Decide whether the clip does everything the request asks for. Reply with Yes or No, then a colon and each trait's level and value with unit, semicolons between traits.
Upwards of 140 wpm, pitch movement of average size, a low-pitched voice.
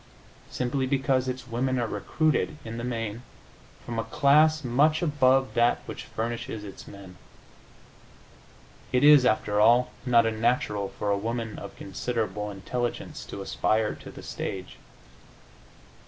No: slow, 135 wpm; average, 3.4 semitones; low, 120 Hz